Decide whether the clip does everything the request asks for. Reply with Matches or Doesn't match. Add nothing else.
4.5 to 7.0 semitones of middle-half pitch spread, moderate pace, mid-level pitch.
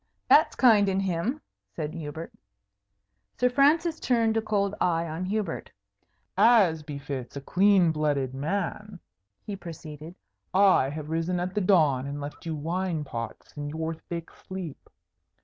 Matches